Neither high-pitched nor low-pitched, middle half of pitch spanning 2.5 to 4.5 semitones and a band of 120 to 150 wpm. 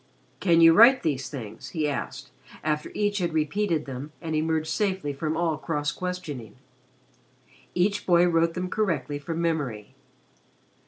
Yes: medium, 160 Hz; average, 3.5 semitones; average, 145 wpm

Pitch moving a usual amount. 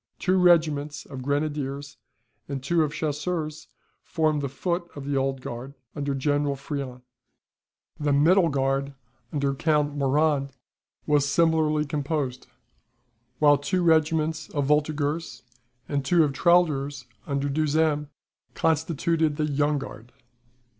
No: narrow, 2.1 semitones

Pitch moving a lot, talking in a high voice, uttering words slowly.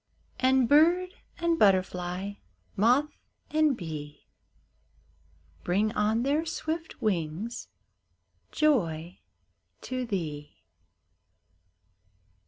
Yes: wide, 9.0 semitones; high, 220 Hz; slow, 70 wpm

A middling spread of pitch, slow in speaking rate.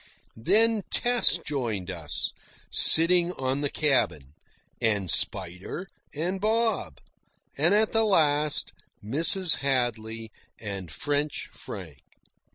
No: wide, 9.0 semitones; slow, 100 wpm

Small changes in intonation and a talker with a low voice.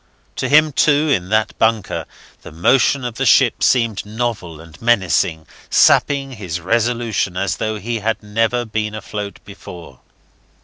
No: average, 3.6 semitones; low, 110 Hz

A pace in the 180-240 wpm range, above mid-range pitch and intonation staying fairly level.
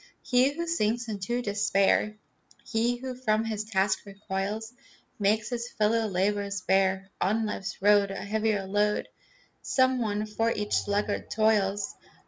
No: slow, 135 wpm; high, 210 Hz; narrow, 2.2 semitones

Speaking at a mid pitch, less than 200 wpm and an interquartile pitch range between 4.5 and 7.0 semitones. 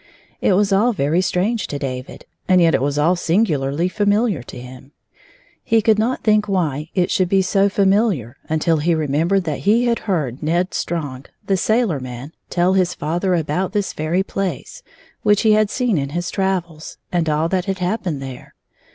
Yes: medium, 180 Hz; average, 190 wpm; average, 4.9 semitones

